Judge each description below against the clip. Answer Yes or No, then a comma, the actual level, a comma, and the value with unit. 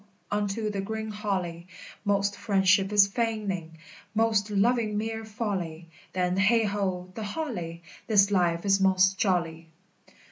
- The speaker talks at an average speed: No, slow, 130 wpm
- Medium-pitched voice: No, high, 200 Hz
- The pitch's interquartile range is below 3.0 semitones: Yes, narrow, 2.6 semitones